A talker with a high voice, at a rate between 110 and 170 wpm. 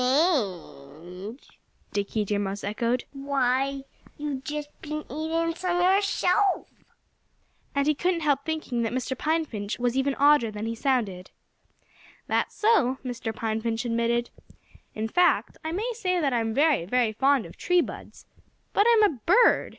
Yes: very high, 270 Hz; average, 150 wpm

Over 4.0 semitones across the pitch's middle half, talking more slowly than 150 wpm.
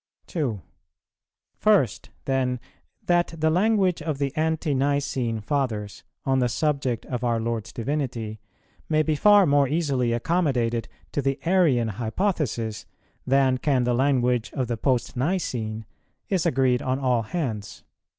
Yes: average, 4.5 semitones; slow, 135 wpm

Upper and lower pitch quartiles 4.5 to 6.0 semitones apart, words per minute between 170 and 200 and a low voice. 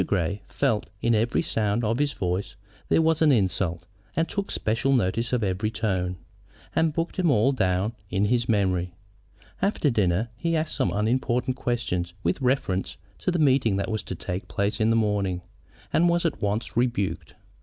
Yes: average, 5.3 semitones; average, 180 wpm; low, 110 Hz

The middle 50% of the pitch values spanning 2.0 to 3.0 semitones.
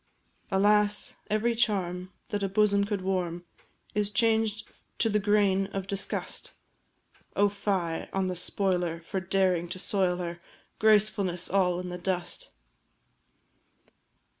Yes: narrow, 2.5 semitones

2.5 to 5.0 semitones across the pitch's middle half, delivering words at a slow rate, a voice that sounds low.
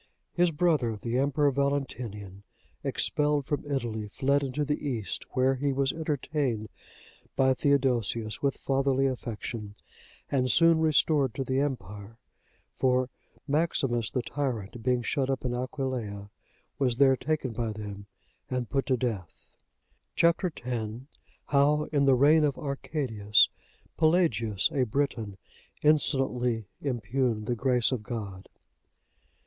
Yes: average, 3.7 semitones; slow, 125 wpm; low, 130 Hz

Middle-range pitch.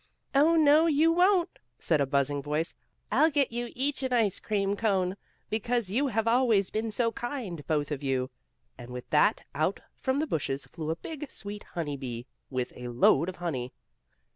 No: high, 200 Hz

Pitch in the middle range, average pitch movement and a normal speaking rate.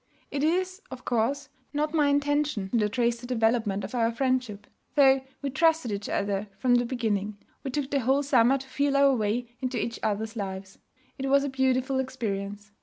No: very high, 250 Hz; average, 4.1 semitones; average, 185 wpm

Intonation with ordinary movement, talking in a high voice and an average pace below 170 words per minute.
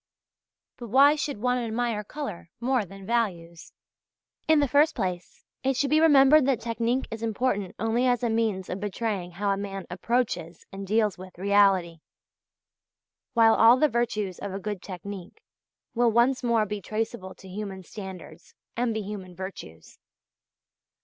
Yes: average, 4.2 semitones; high, 215 Hz; average, 155 wpm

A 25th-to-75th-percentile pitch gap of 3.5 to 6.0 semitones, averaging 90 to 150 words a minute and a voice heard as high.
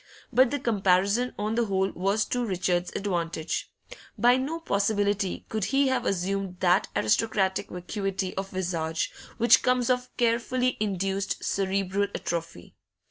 Yes: average, 4.2 semitones; slow, 135 wpm; high, 195 Hz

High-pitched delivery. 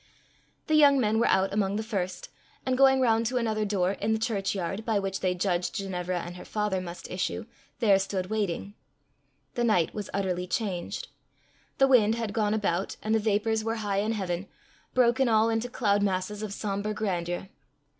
Yes: high, 210 Hz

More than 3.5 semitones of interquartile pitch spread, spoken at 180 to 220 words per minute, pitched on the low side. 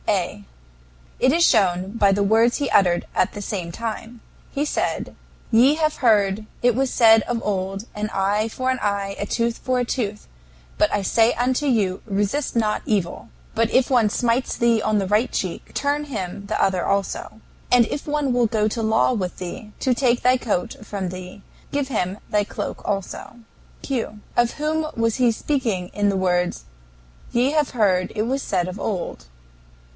No: average, 3.9 semitones; average, 185 wpm; high, 220 Hz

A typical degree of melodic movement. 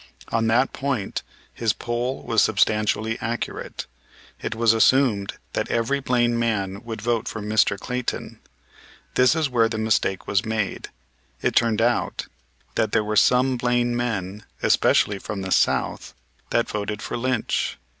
No: narrow, 2.3 semitones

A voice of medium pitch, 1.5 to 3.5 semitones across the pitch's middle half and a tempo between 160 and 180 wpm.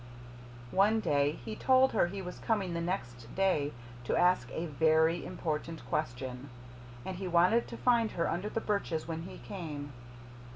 No: medium, 170 Hz; average, 4.7 semitones; average, 165 wpm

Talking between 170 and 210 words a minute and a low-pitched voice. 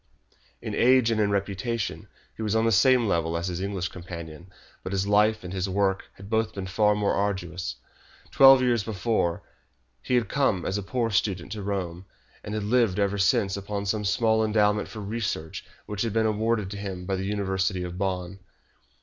Yes: average, 190 wpm; low, 100 Hz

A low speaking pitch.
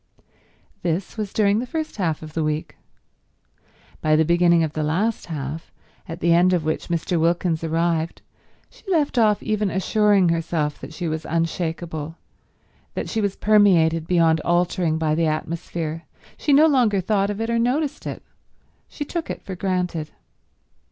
No: medium, 170 Hz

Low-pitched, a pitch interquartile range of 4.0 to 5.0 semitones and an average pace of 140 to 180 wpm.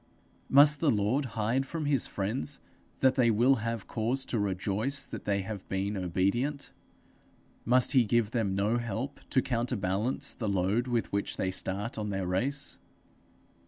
Yes: low, 115 Hz; average, 4.7 semitones; average, 160 wpm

